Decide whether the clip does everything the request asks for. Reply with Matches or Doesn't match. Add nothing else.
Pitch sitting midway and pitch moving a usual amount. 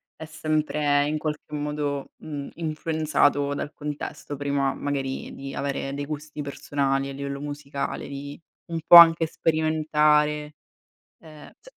Doesn't match